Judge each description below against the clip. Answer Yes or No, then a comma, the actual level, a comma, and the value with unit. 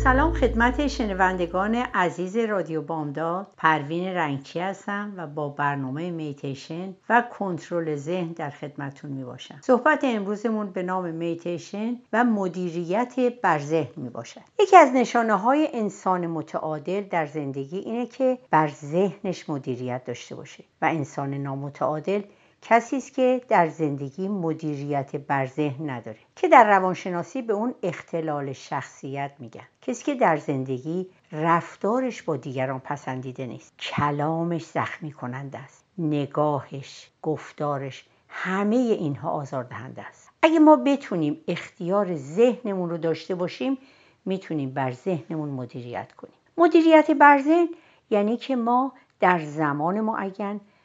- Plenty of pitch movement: Yes, wide, 6.6 semitones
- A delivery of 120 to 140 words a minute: Yes, average, 130 wpm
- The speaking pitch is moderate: Yes, medium, 170 Hz